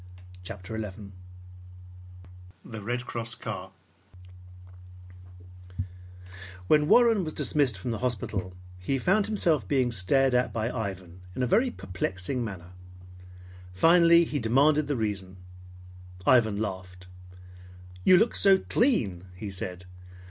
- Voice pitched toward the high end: No, low, 115 Hz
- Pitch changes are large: Yes, wide, 7.7 semitones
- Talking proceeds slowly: Yes, slow, 115 wpm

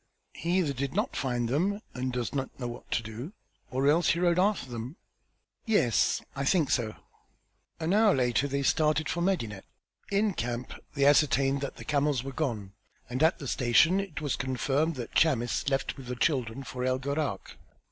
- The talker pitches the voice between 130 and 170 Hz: Yes, medium, 140 Hz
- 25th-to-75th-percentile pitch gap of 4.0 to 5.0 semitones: Yes, average, 4.3 semitones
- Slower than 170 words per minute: No, average, 180 wpm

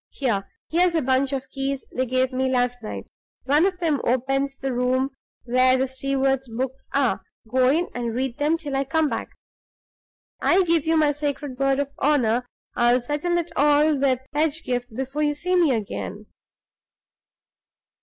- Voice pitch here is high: Yes, very high, 270 Hz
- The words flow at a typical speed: Yes, average, 165 wpm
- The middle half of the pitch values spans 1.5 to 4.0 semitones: Yes, average, 2.7 semitones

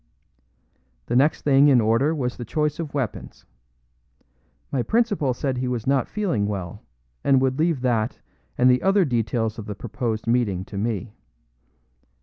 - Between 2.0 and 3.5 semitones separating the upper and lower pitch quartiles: No, average, 4.1 semitones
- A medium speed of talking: Yes, average, 155 wpm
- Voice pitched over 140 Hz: No, low, 125 Hz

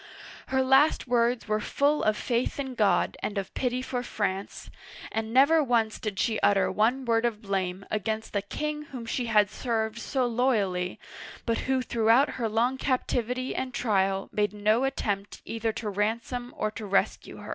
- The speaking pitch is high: Yes, high, 230 Hz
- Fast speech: No, average, 175 wpm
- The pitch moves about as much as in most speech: Yes, average, 3.3 semitones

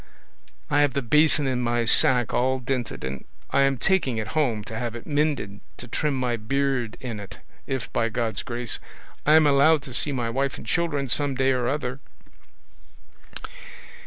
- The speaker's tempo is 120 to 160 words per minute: No, average, 180 wpm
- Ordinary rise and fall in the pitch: Yes, average, 3.0 semitones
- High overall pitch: No, low, 130 Hz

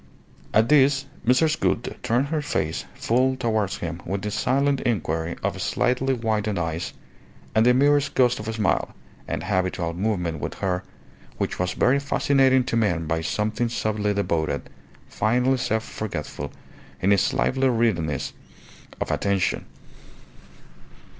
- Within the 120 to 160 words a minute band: Yes, average, 140 wpm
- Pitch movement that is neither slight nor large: No, wide, 6.0 semitones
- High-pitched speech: No, low, 110 Hz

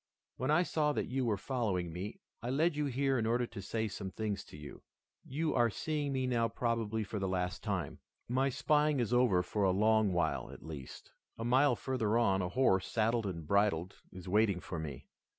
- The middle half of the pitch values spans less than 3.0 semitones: No, average, 5.3 semitones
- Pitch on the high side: No, low, 110 Hz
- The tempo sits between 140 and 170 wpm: No, fast, 205 wpm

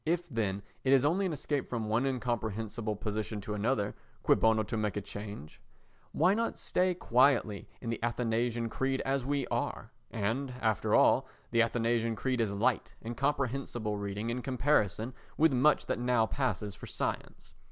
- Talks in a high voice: No, low, 120 Hz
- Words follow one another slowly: No, average, 170 wpm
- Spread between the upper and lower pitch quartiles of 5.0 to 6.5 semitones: No, average, 3.7 semitones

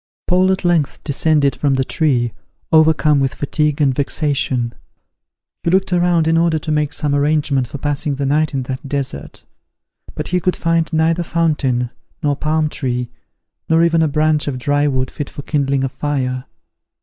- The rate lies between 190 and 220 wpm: No, average, 175 wpm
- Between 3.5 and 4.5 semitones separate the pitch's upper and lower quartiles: No, average, 2.8 semitones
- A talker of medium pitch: Yes, medium, 150 Hz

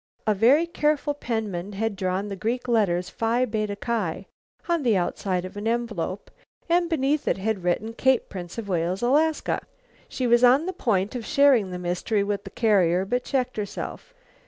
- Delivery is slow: No, average, 185 wpm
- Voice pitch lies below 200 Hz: No, high, 220 Hz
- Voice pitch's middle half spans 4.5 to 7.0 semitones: Yes, average, 4.9 semitones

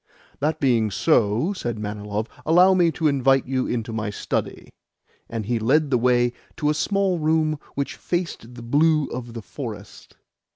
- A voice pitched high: No, low, 130 Hz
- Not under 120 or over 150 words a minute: No, average, 165 wpm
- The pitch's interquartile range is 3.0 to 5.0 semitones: No, wide, 5.4 semitones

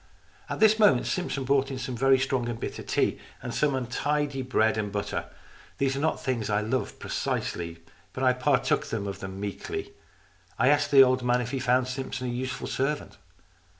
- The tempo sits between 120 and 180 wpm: No, average, 190 wpm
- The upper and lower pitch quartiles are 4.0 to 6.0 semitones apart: No, average, 2.7 semitones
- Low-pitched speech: Yes, low, 130 Hz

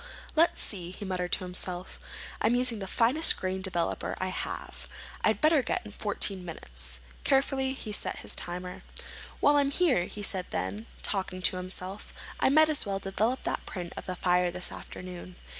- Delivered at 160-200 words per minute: Yes, average, 180 wpm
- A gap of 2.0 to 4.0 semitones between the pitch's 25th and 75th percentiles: No, wide, 5.4 semitones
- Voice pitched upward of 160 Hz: Yes, high, 190 Hz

